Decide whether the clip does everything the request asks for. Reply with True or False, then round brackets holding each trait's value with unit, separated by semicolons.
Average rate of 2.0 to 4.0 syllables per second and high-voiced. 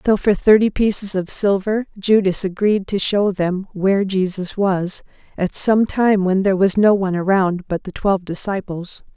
False (4.8 syllables/s; 195 Hz)